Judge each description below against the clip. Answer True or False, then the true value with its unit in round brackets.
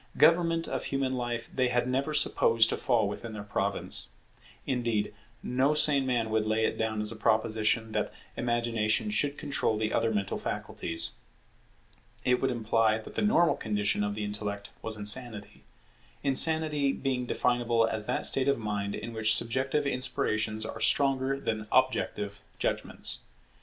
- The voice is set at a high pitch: False (115 Hz)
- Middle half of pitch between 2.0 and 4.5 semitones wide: True (3.6 semitones)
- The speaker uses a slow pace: False (155 wpm)